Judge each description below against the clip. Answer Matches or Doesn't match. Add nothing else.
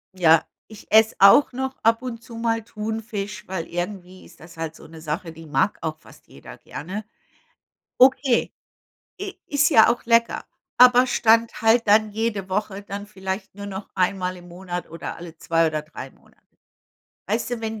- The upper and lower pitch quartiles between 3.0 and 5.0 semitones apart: Matches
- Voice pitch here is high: Matches